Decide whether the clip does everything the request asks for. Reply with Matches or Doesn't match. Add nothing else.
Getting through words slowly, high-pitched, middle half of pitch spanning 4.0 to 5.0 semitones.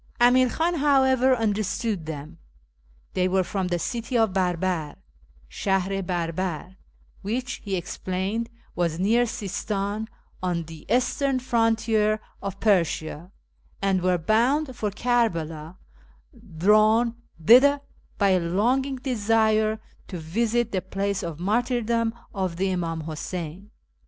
Matches